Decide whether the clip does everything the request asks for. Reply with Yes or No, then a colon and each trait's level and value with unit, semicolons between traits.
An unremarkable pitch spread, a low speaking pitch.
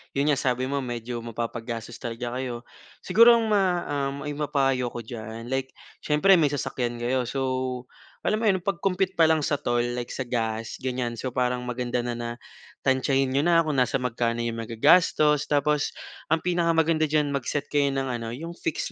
Yes: average, 3.9 semitones; low, 130 Hz